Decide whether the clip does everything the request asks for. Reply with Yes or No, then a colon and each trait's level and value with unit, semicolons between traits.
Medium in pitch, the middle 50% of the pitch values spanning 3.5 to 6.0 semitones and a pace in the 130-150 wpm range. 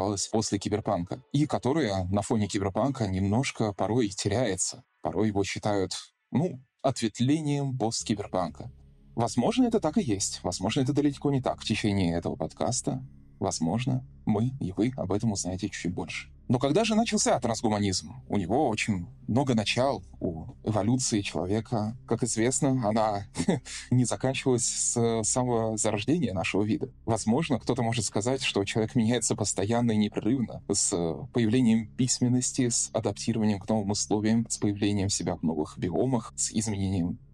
No: low, 110 Hz; average, 4.0 semitones; average, 145 wpm